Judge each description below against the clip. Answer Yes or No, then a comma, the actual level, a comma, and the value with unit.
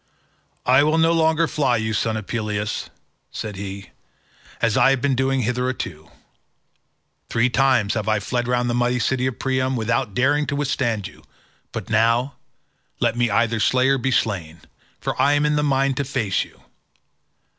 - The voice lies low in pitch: Yes, low, 125 Hz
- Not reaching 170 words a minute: No, average, 175 wpm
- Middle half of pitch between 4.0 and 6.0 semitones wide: No, average, 3.5 semitones